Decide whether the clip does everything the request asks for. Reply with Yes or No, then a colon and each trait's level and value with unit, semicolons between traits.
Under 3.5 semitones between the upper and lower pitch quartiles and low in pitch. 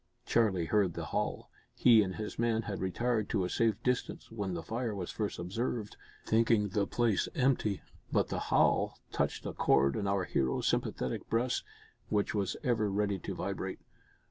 Yes: average, 3.1 semitones; low, 105 Hz